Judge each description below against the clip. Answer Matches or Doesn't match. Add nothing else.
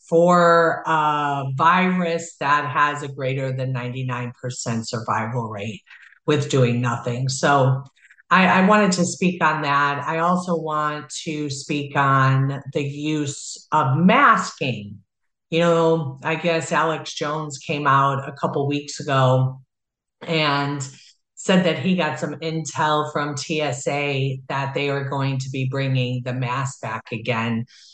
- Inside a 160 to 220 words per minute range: Doesn't match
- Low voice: Doesn't match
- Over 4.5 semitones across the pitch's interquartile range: Doesn't match